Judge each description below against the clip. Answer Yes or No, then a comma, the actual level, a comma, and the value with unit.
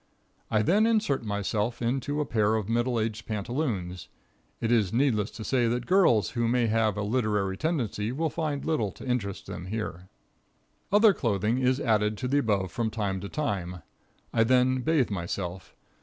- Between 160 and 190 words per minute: Yes, average, 170 wpm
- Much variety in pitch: No, average, 3.9 semitones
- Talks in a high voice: No, low, 115 Hz